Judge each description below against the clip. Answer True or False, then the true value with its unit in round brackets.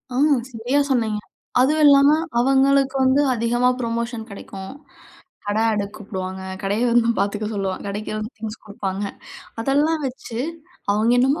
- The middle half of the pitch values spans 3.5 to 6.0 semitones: True (4.2 semitones)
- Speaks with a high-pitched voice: True (230 Hz)